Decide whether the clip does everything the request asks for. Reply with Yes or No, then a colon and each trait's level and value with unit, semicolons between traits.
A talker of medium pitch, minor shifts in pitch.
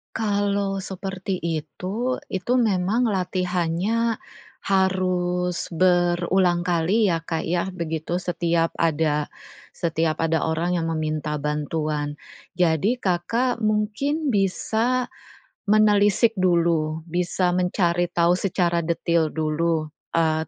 No: medium, 175 Hz; average, 3.1 semitones